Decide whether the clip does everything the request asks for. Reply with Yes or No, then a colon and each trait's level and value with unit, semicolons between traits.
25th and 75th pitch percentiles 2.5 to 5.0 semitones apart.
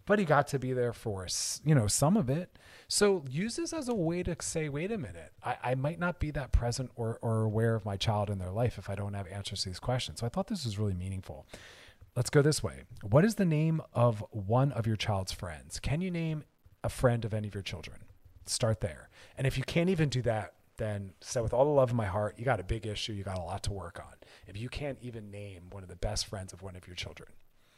No: wide, 5.4 semitones